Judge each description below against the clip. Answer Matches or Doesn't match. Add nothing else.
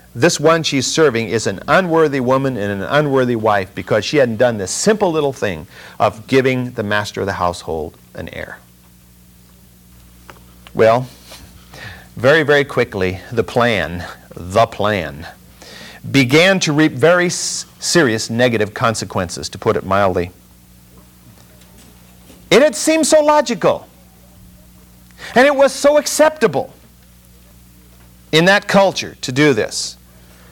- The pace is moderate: Doesn't match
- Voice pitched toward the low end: Matches